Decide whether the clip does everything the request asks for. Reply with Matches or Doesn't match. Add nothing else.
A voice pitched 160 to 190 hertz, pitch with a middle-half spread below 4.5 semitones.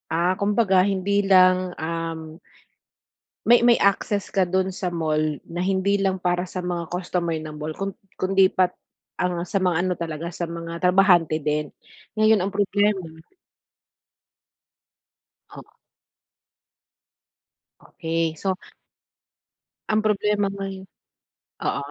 Matches